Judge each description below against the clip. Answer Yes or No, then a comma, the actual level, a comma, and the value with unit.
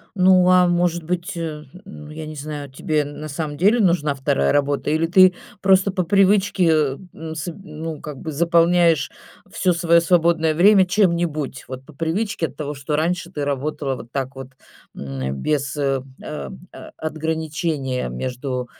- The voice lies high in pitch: No, medium, 155 Hz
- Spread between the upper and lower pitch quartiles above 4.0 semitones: No, average, 3.5 semitones